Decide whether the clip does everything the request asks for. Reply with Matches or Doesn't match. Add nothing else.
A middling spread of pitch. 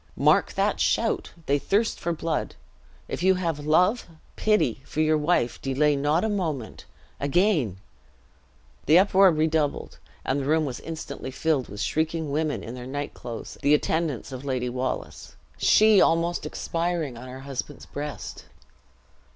Matches